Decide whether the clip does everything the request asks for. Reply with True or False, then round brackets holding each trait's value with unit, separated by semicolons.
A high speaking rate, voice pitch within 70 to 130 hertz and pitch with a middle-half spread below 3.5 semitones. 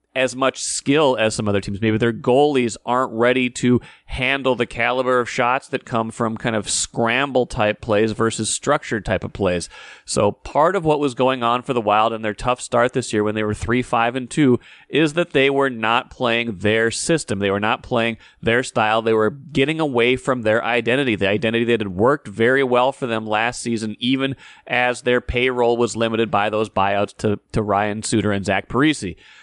True (210 wpm; 115 Hz; 2.9 semitones)